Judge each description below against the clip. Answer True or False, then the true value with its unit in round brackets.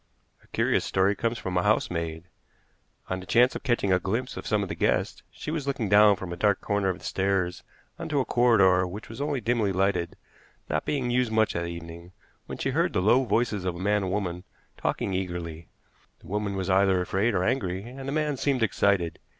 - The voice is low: True (100 Hz)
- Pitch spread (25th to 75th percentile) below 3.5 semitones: False (4.3 semitones)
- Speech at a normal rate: False (215 wpm)